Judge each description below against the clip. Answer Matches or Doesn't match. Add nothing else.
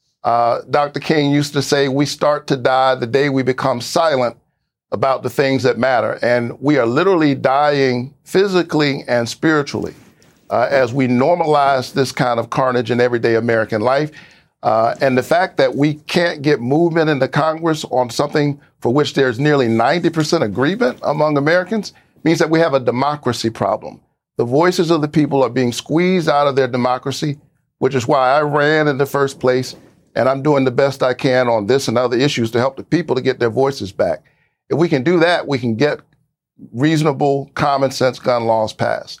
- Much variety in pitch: Doesn't match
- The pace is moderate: Matches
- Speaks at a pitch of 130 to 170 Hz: Matches